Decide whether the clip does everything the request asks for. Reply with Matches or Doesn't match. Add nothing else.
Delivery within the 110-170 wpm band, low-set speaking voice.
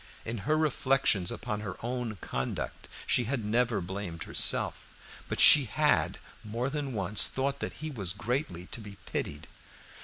Matches